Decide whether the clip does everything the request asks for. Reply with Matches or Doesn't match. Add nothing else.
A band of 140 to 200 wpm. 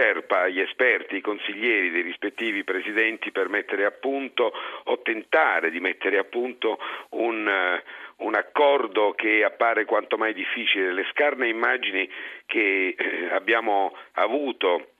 Doesn't match